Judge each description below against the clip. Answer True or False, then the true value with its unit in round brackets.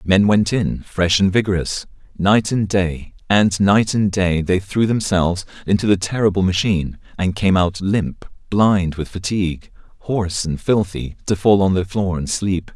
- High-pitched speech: False (95 Hz)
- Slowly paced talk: False (175 wpm)